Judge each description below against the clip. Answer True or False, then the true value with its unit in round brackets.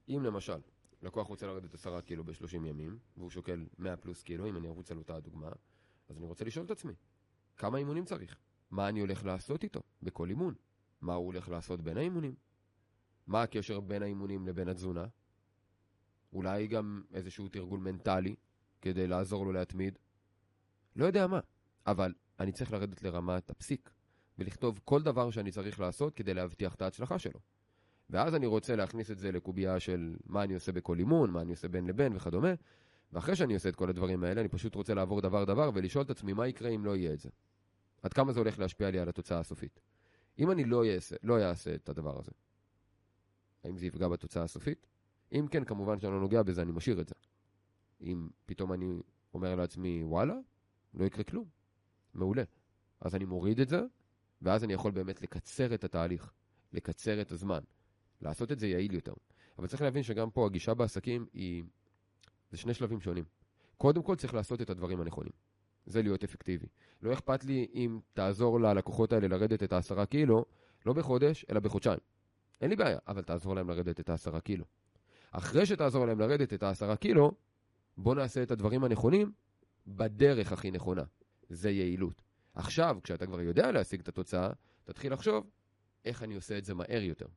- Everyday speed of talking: False (180 wpm)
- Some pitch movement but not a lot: True (3.6 semitones)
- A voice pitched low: True (100 Hz)